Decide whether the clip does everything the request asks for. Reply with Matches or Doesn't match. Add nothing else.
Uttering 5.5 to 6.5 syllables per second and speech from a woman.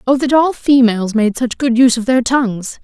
Matches